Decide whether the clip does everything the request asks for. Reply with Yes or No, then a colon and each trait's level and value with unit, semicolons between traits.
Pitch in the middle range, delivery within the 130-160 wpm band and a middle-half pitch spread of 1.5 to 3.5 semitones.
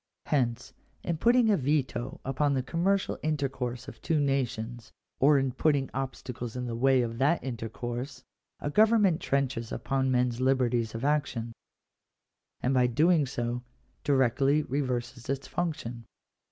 No: low, 130 Hz; average, 145 wpm; average, 3.1 semitones